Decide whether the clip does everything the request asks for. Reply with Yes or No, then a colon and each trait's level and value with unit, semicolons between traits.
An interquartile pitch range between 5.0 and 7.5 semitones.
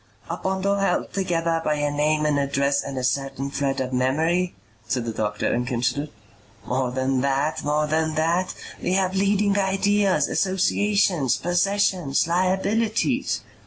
Yes: wide, 5.6 semitones